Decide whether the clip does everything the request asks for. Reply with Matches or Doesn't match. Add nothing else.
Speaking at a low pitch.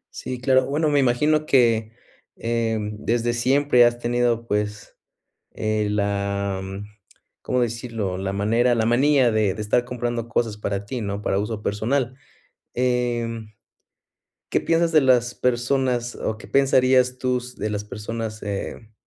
Matches